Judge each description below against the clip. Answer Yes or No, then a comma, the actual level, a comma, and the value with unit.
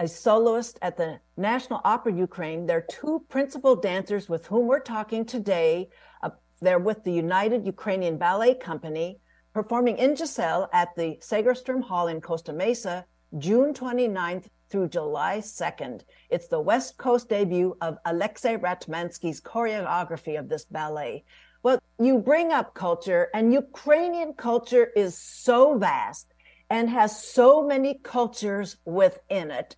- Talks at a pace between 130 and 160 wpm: Yes, average, 140 wpm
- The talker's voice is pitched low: No, high, 215 Hz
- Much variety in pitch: Yes, wide, 6.2 semitones